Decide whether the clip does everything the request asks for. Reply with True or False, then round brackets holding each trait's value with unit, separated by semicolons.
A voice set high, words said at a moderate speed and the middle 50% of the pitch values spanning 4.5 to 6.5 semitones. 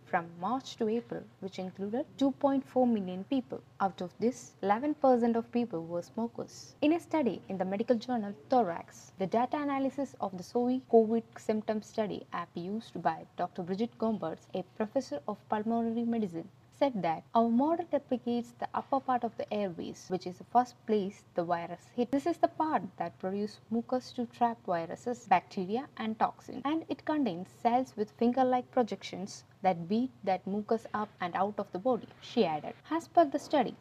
True (230 Hz; 180 wpm; 4.9 semitones)